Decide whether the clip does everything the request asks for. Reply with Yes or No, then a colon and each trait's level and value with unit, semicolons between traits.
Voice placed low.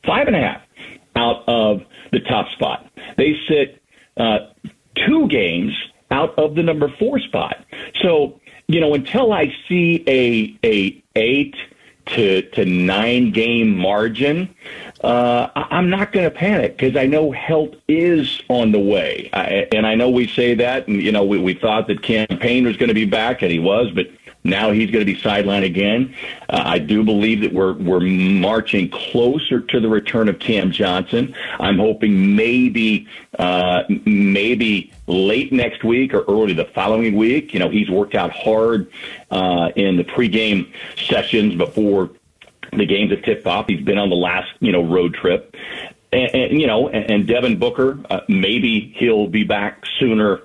Yes: low, 110 Hz